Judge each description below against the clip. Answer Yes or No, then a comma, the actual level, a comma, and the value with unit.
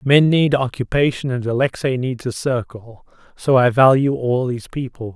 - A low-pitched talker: Yes, low, 130 Hz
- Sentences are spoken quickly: No, average, 165 wpm